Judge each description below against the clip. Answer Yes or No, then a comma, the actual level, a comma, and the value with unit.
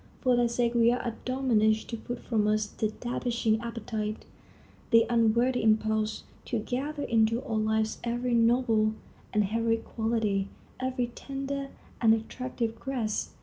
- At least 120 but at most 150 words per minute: Yes, average, 140 wpm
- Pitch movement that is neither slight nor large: No, narrow, 2.1 semitones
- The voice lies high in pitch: Yes, high, 230 Hz